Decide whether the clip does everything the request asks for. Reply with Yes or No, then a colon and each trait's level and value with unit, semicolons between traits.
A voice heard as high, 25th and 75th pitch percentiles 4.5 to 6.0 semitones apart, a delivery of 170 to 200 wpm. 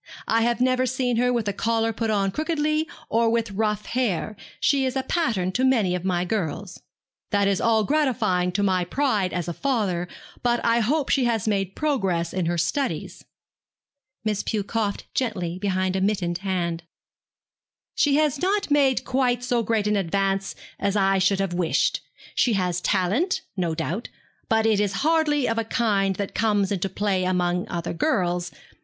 Yes: high, 210 Hz; average, 4.9 semitones; average, 175 wpm